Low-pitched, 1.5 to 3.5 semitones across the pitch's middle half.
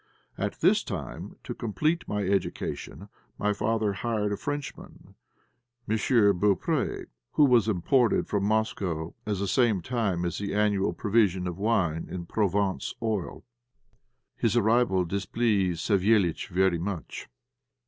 Yes: low, 100 Hz; average, 3.1 semitones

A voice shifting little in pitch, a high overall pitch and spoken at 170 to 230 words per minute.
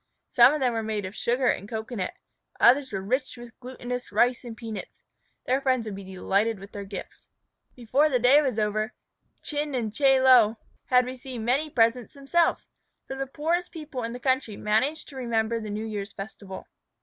No: average, 3.4 semitones; high, 240 Hz; average, 185 wpm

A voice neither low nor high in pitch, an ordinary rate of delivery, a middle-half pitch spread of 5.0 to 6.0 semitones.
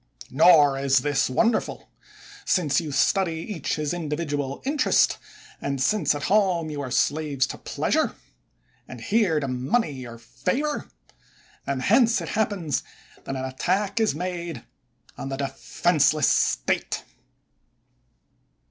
No: medium, 155 Hz; slow, 125 wpm; wide, 5.4 semitones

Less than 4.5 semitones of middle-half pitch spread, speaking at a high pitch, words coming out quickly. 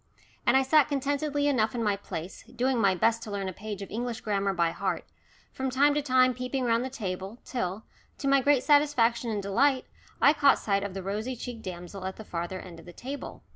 No: average, 5.2 semitones; high, 230 Hz; fast, 220 wpm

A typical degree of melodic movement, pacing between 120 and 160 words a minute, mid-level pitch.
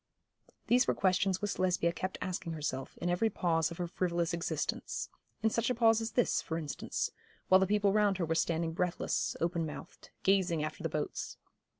No: average, 3.1 semitones; average, 190 wpm; medium, 180 Hz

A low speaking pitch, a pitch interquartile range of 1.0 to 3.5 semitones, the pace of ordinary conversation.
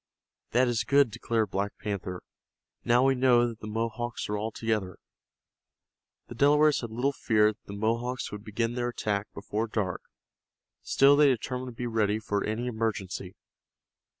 Yes: low, 115 Hz; narrow, 2.6 semitones; average, 160 wpm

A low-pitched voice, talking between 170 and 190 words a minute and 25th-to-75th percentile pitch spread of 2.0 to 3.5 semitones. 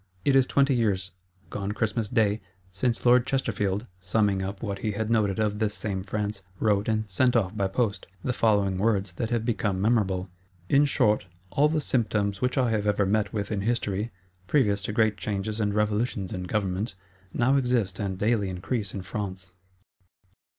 Yes: low, 105 Hz; average, 180 wpm; average, 2.7 semitones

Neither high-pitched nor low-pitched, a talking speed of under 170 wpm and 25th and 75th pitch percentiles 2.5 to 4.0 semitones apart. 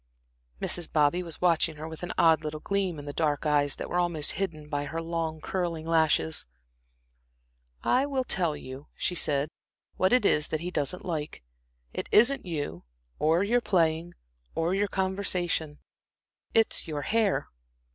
Yes: medium, 165 Hz; average, 160 wpm; average, 3.4 semitones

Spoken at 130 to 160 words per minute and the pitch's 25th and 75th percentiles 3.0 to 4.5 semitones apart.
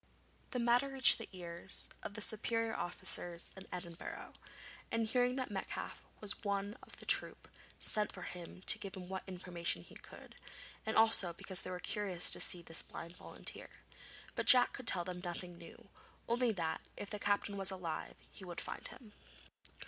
No: average, 180 wpm; average, 4.0 semitones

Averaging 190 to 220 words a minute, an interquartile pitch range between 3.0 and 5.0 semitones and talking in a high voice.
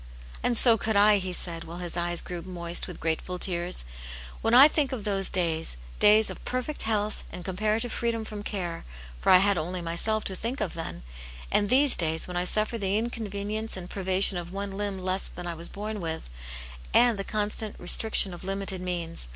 Yes: fast, 205 wpm; average, 3.6 semitones; high, 195 Hz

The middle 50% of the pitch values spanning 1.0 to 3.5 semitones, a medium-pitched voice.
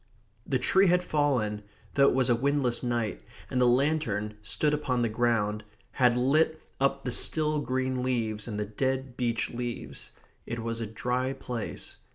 No: average, 3.1 semitones; low, 125 Hz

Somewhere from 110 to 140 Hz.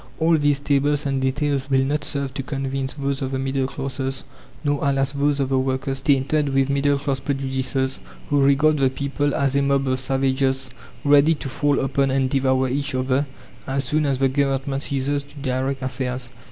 Yes: low, 135 Hz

